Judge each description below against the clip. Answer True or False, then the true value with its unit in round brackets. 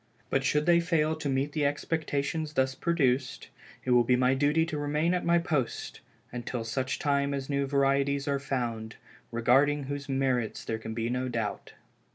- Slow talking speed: False (180 wpm)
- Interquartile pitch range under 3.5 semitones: True (2.8 semitones)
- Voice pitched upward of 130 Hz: True (140 Hz)